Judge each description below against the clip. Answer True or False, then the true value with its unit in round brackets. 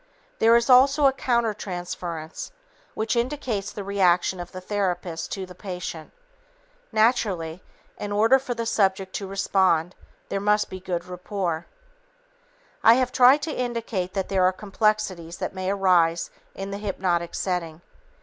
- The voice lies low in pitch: False (195 Hz)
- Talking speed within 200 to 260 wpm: False (145 wpm)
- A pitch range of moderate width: True (3.8 semitones)